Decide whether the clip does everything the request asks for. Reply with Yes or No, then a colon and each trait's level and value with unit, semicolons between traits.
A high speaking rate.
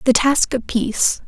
No: average, 190 wpm